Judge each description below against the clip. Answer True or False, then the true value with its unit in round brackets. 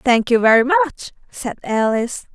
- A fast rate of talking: False (155 wpm)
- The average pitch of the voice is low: False (255 Hz)